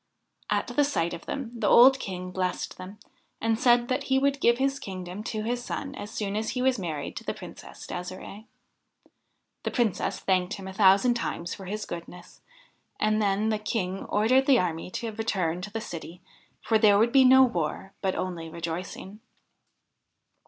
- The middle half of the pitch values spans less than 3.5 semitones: No, average, 4.6 semitones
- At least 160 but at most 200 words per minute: Yes, average, 180 wpm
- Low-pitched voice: No, high, 210 Hz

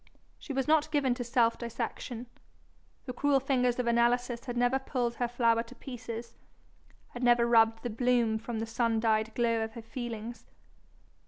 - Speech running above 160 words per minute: Yes, average, 170 wpm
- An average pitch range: No, narrow, 1.4 semitones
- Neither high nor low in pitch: No, high, 240 Hz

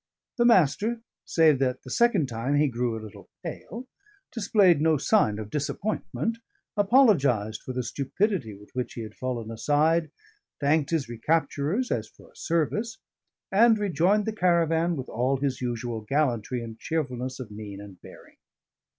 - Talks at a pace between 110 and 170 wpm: Yes, average, 155 wpm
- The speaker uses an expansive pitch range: Yes, wide, 7.3 semitones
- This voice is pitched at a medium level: Yes, medium, 145 Hz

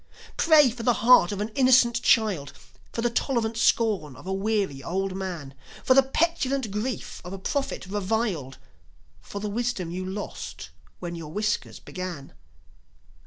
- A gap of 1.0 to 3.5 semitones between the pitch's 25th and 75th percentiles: No, average, 4.6 semitones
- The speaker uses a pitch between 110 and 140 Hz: No, high, 210 Hz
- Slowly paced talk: No, average, 155 wpm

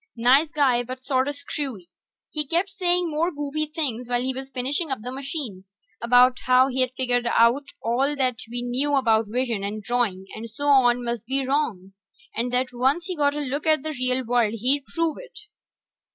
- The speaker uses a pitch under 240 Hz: No, very high, 260 Hz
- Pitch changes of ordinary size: Yes, average, 3.1 semitones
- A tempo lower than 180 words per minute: No, average, 190 wpm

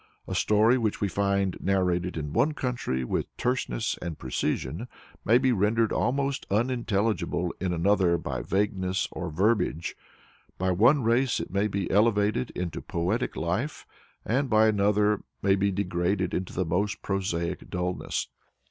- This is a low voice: Yes, low, 100 Hz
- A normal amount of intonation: Yes, average, 3.8 semitones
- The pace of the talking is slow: No, average, 145 wpm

